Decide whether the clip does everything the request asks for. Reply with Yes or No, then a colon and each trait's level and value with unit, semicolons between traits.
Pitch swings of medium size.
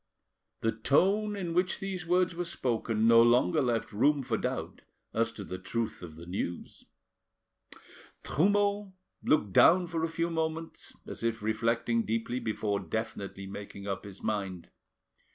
No: wide, 7.8 semitones